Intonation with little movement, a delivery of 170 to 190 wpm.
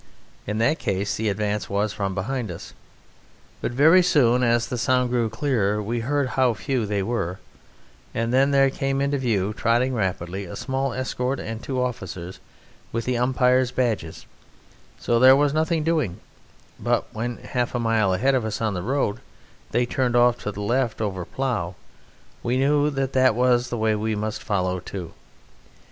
No: average, 3.9 semitones; average, 175 wpm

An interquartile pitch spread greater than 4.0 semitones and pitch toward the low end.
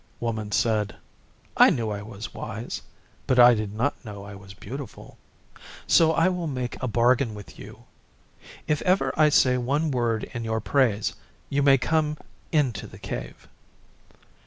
Yes: average, 4.7 semitones; low, 120 Hz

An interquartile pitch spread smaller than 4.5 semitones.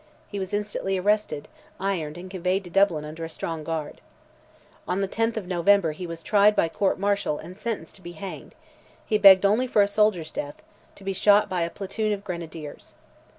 Yes: average, 3.4 semitones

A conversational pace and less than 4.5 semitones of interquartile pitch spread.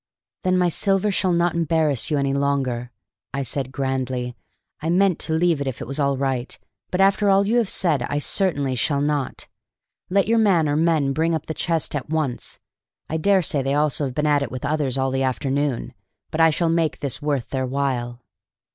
No: fast, 210 wpm; average, 3.9 semitones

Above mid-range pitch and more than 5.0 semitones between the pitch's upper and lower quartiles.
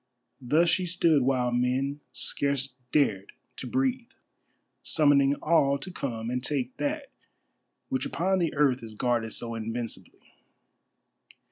No: medium, 140 Hz; wide, 5.4 semitones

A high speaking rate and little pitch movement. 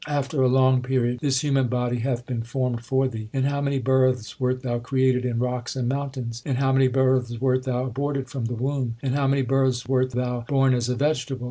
Yes: fast, 230 wpm; narrow, 1.4 semitones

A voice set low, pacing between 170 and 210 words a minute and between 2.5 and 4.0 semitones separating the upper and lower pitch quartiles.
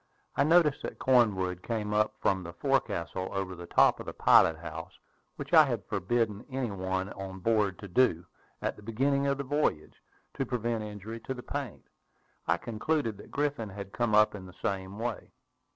No: low, 105 Hz; average, 185 wpm; average, 4.7 semitones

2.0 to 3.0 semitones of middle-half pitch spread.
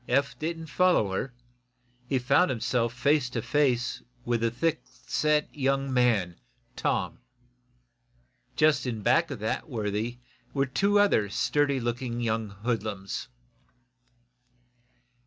No: average, 4.3 semitones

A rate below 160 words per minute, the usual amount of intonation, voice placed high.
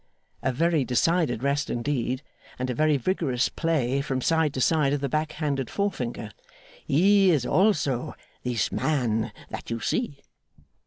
No: average, 150 wpm; average, 4.4 semitones; medium, 140 Hz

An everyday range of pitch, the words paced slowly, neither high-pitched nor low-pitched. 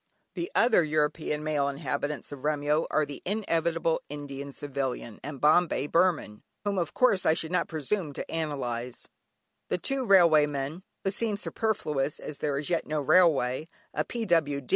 No: average, 3.7 semitones; average, 160 wpm; medium, 155 Hz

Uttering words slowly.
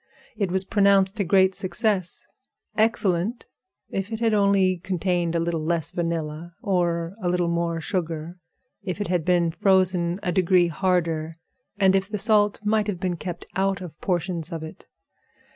No: average, 160 wpm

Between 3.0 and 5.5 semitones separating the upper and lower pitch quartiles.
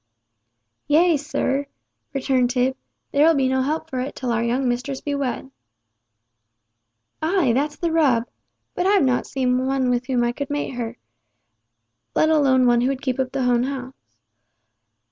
No: narrow, 2.5 semitones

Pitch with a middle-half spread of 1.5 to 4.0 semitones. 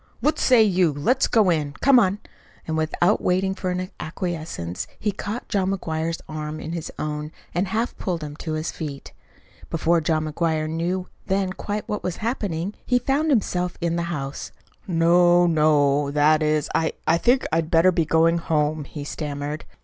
Yes: average, 3.3 semitones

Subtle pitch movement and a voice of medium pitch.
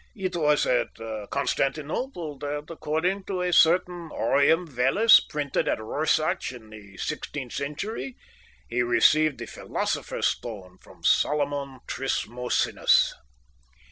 No: average, 4.5 semitones; medium, 145 Hz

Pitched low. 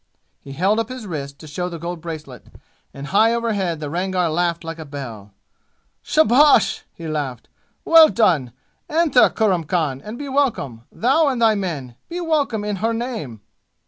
No: medium, 180 Hz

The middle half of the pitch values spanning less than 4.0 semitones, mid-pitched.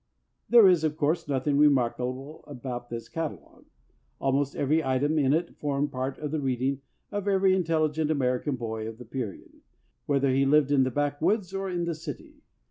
Yes: average, 3.5 semitones; medium, 145 Hz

